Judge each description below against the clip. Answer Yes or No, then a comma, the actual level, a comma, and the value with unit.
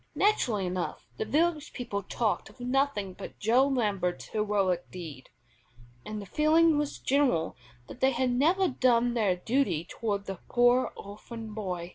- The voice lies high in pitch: Yes, high, 230 Hz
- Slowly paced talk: No, average, 150 wpm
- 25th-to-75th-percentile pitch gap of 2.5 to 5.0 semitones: No, wide, 5.5 semitones